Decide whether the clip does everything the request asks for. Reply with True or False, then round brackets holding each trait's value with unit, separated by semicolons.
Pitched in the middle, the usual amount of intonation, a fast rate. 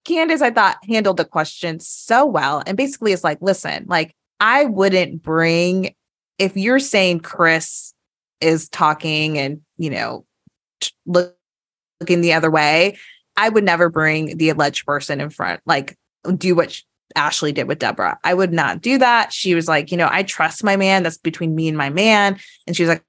False (170 Hz; 3.4 semitones; 185 wpm)